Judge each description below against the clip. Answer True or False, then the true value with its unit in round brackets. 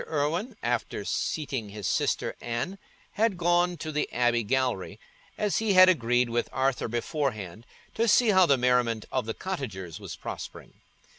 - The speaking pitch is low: True (130 Hz)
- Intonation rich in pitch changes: True (7.2 semitones)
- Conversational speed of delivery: True (155 wpm)